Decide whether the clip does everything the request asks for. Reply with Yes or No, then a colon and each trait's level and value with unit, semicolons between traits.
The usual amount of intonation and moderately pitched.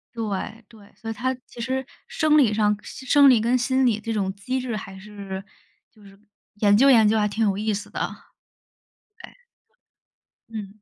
No: average, 3.4 semitones; high, 220 Hz